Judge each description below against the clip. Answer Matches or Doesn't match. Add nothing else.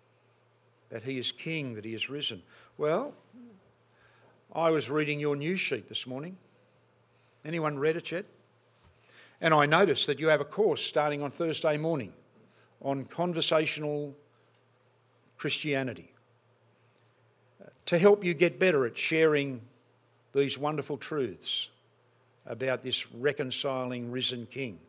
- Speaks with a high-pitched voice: Doesn't match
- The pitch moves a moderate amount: Matches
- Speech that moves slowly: Matches